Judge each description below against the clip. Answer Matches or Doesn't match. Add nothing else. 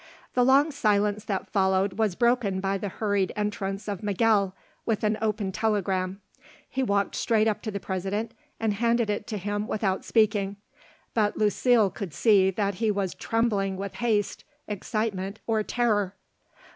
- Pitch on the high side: Matches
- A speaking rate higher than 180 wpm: Doesn't match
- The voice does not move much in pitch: Matches